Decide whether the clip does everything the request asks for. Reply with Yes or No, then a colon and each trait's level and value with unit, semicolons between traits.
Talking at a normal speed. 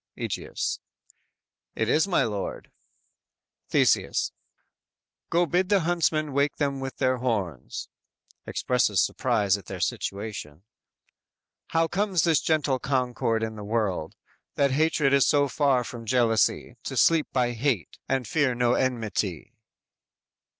No: slow, 130 wpm